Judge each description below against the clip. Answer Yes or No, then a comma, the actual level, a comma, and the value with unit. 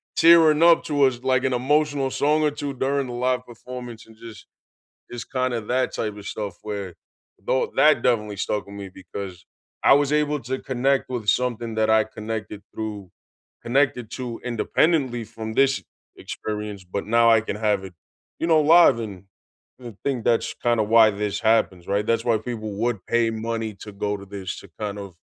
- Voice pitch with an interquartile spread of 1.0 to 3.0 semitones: No, average, 3.6 semitones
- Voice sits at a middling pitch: No, low, 115 Hz